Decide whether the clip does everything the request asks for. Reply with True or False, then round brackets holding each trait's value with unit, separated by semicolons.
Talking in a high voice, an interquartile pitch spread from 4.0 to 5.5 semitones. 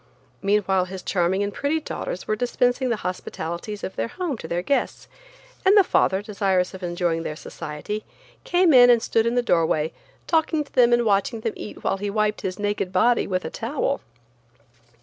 True (205 Hz; 4.9 semitones)